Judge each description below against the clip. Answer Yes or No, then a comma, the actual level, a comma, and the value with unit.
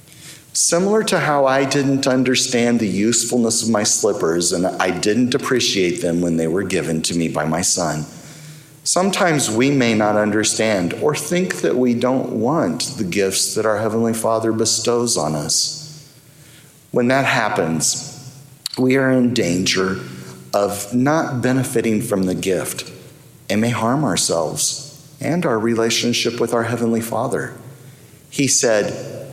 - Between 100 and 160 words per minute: Yes, average, 145 wpm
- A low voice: Yes, low, 120 Hz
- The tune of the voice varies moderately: Yes, average, 5.0 semitones